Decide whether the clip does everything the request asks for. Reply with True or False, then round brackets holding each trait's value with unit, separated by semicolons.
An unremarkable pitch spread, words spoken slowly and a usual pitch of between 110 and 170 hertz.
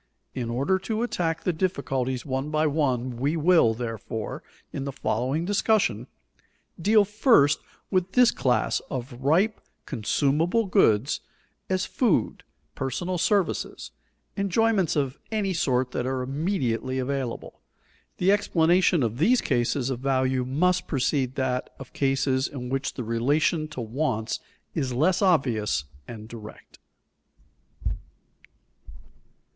False (6.2 semitones; 120 wpm; 140 Hz)